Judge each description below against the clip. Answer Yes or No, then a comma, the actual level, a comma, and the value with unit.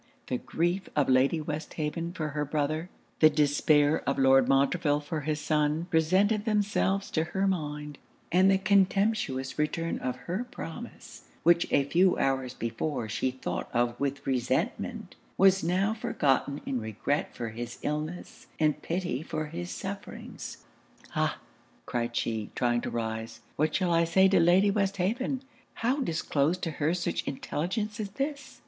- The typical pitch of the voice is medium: Yes, medium, 155 Hz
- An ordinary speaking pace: Yes, average, 150 wpm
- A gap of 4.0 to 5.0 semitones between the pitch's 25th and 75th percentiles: No, wide, 5.5 semitones